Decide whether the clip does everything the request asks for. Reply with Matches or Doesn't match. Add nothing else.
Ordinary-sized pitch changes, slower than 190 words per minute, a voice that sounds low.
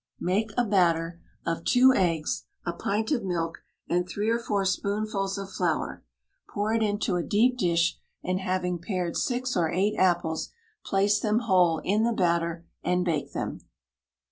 Doesn't match